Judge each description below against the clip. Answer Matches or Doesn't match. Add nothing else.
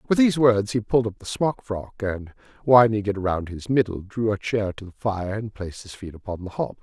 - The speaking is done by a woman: Doesn't match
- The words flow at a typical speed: Doesn't match